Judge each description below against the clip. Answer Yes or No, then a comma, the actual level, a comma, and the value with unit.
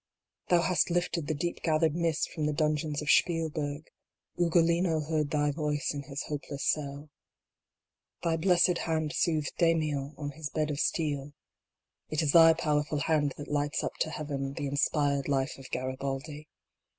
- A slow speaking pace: No, average, 160 wpm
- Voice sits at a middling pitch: Yes, medium, 150 Hz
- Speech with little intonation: Yes, narrow, 2.2 semitones